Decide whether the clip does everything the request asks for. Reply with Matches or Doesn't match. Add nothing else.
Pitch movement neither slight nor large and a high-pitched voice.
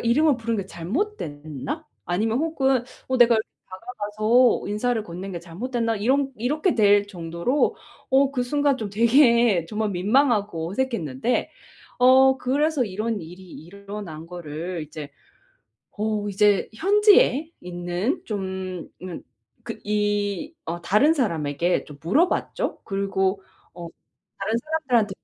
Doesn't match